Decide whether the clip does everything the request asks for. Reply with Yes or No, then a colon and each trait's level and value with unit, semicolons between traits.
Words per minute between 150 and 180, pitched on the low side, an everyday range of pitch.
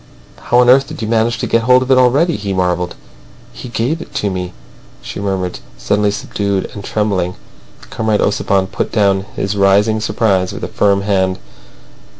Yes: average, 175 wpm; low, 105 Hz; average, 3.0 semitones